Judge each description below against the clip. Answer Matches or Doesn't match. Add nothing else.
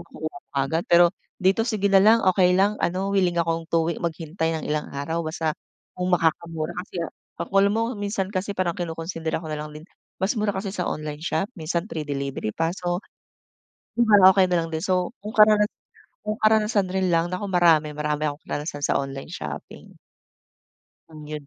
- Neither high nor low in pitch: Matches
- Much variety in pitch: Doesn't match